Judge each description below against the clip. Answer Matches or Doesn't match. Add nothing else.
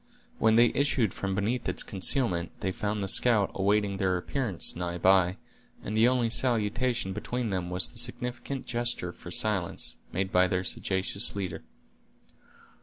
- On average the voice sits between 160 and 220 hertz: Doesn't match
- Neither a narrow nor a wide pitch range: Matches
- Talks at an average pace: Matches